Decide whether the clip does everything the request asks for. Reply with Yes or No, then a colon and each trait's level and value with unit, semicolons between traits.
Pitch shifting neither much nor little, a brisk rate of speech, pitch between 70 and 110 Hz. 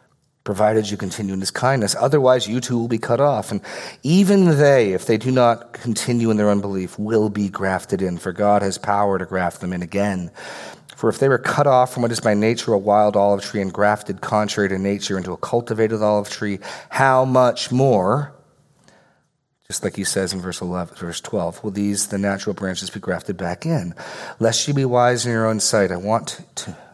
Yes: average, 3.6 semitones; fast, 210 wpm; low, 105 Hz